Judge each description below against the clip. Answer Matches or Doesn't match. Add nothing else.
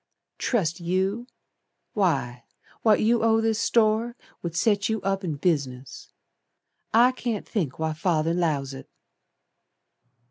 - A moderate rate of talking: Doesn't match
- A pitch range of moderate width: Doesn't match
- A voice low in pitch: Doesn't match